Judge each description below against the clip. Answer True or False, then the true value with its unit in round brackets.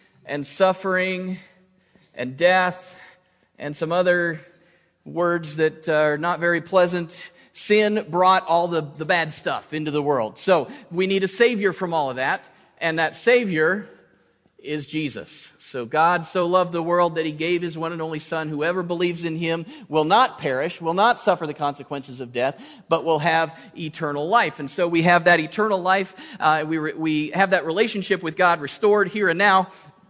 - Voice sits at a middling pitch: True (170 Hz)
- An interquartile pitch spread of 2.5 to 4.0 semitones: True (2.8 semitones)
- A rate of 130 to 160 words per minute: False (180 wpm)